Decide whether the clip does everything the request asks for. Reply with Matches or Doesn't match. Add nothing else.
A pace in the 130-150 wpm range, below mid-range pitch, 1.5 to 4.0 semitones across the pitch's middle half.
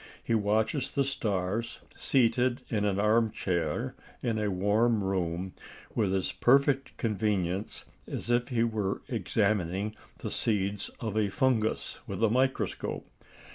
Matches